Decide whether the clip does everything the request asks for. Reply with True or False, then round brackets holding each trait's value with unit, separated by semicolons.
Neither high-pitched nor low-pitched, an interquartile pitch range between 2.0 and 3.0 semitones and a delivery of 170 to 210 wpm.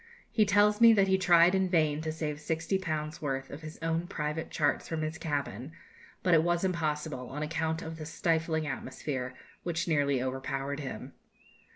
True (160 Hz; 2.6 semitones; 180 wpm)